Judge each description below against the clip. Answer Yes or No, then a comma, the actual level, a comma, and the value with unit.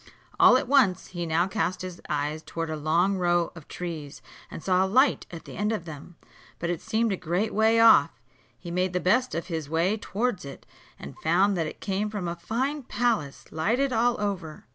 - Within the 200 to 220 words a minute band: Yes, fast, 205 wpm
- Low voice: No, medium, 180 Hz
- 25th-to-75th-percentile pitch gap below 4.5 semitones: No, average, 4.9 semitones